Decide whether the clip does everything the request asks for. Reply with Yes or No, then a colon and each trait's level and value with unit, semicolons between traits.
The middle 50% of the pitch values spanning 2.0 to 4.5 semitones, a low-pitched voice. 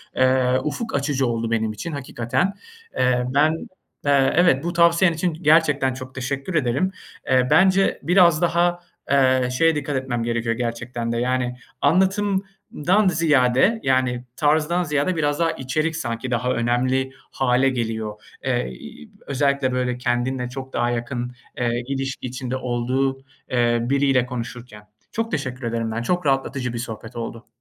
Yes: average, 4.0 semitones; low, 130 Hz